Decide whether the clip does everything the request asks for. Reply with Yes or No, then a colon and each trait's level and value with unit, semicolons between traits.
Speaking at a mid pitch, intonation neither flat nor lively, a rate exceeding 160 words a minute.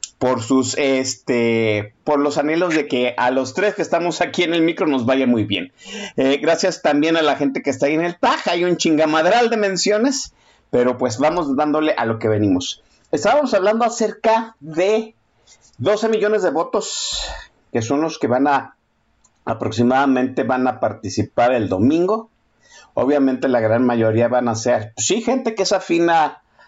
No: medium, 145 Hz; wide, 6.3 semitones; average, 180 wpm